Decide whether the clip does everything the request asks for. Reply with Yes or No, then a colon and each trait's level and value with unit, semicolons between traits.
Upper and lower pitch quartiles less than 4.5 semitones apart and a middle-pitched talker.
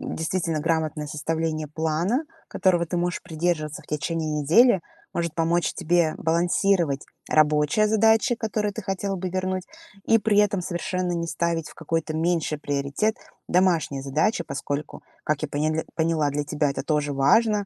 Yes: average, 3.4 semitones; medium, 165 Hz